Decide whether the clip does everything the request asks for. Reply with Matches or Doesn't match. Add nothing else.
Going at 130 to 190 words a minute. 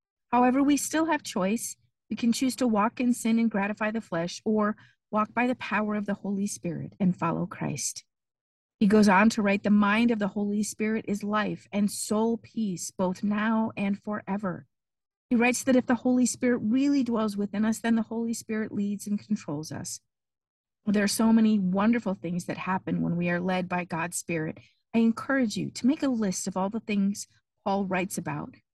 Doesn't match